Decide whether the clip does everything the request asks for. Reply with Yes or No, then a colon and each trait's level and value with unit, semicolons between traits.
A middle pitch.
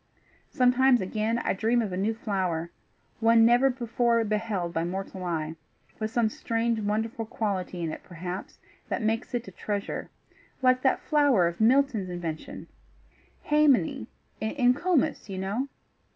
No: high, 220 Hz